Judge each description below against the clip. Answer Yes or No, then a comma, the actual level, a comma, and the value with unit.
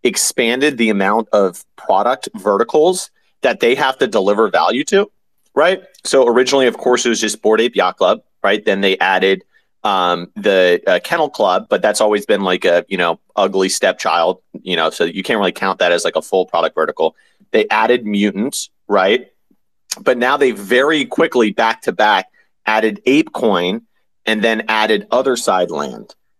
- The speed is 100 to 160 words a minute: No, average, 180 wpm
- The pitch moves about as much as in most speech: Yes, average, 3.4 semitones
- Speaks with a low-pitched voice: Yes, low, 110 Hz